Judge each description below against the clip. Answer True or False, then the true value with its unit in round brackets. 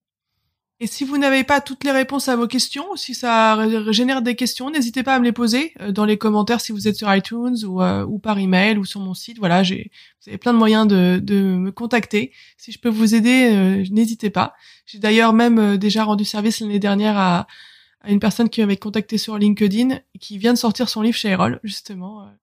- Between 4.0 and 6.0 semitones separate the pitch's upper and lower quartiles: False (3.0 semitones)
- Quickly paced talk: True (230 wpm)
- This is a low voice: False (220 Hz)